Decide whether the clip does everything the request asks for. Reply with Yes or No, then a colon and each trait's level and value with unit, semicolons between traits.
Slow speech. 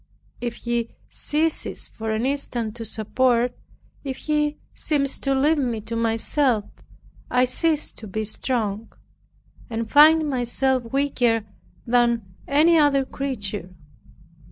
Yes: slow, 120 wpm